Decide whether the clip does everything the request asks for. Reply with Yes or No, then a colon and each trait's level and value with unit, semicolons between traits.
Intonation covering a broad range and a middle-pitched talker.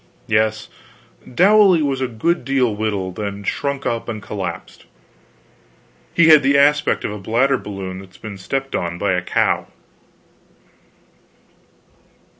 No: wide, 5.7 semitones; low, 110 Hz